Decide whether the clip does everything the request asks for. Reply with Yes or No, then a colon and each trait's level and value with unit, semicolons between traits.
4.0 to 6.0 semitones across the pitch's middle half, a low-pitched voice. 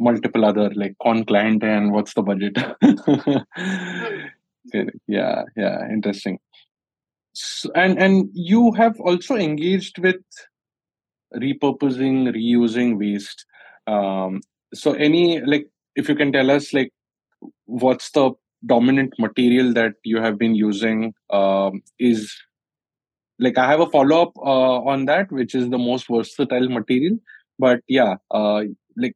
Yes: average, 4.9 semitones; low, 125 Hz